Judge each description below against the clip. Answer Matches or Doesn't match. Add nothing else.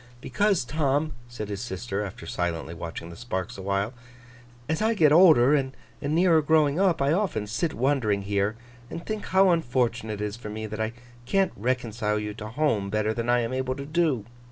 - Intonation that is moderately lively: Doesn't match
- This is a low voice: Matches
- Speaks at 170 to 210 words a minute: Matches